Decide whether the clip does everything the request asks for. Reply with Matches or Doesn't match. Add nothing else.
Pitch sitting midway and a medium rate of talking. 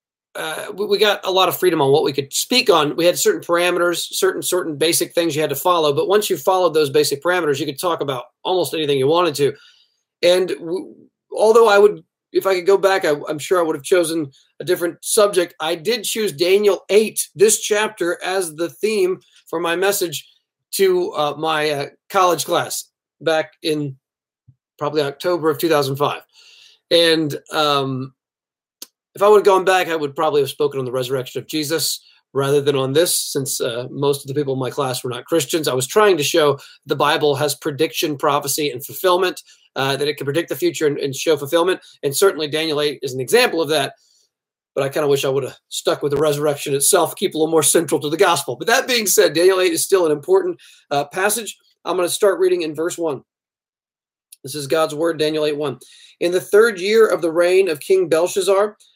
Doesn't match